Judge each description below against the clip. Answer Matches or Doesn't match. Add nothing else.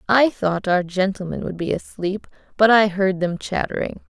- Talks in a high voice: Matches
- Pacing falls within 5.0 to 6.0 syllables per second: Doesn't match